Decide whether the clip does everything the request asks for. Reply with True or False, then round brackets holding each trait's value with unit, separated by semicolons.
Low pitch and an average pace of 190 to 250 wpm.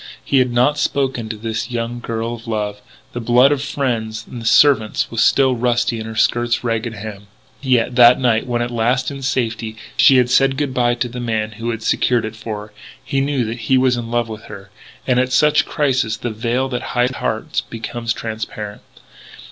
True (120 Hz; 205 wpm)